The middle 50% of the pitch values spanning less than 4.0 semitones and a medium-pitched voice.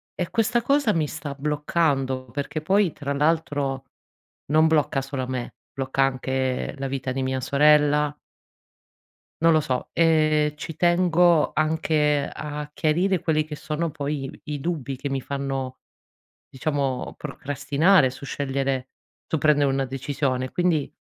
Yes: narrow, 2.6 semitones; medium, 145 Hz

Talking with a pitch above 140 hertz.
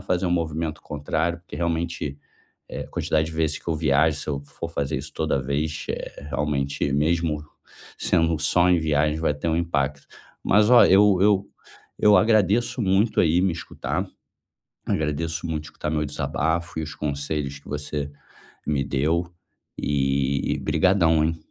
No: very low, 80 Hz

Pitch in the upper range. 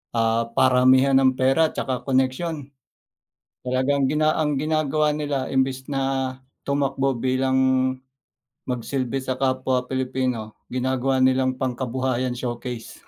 No: low, 130 Hz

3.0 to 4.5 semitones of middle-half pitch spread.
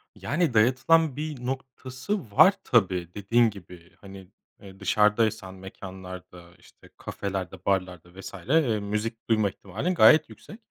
No: average, 5.3 semitones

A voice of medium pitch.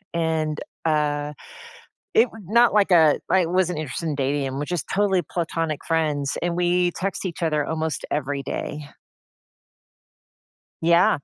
Yes: medium, 160 Hz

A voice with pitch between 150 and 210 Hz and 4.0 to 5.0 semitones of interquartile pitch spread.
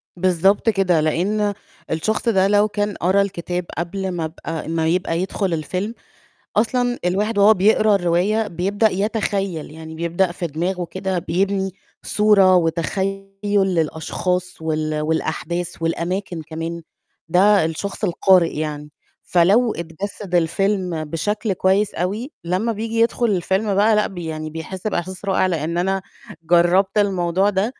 No: medium, 185 Hz; average, 3.2 semitones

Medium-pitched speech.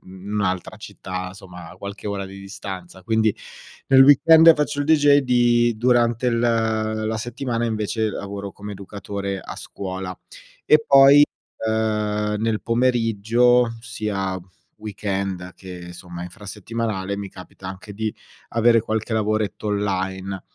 No: low, 105 Hz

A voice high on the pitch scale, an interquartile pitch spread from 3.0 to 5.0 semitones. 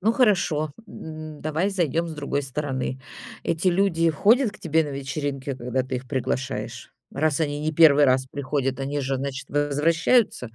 No: medium, 145 Hz; average, 3.3 semitones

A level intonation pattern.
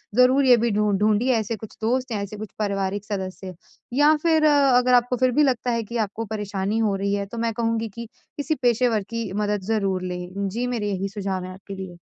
No: average, 3.4 semitones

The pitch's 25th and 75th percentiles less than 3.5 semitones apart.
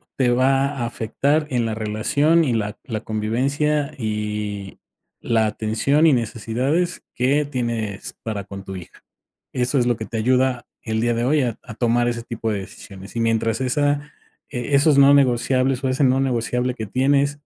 No: average, 3.8 semitones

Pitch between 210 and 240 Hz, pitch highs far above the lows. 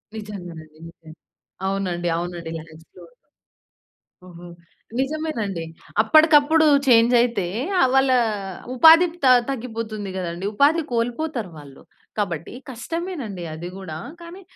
Yes: high, 215 Hz; wide, 7.8 semitones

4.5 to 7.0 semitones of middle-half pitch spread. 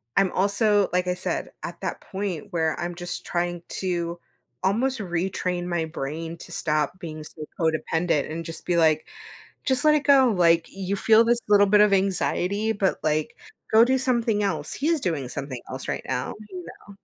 No: average, 4.0 semitones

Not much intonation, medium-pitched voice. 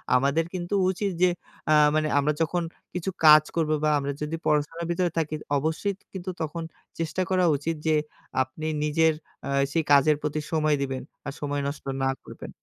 Yes: narrow, 2.3 semitones; medium, 155 Hz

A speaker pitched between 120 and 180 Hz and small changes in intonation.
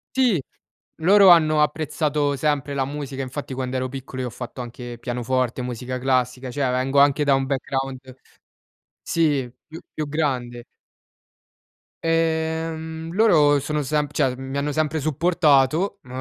No: medium, 140 Hz; average, 3.4 semitones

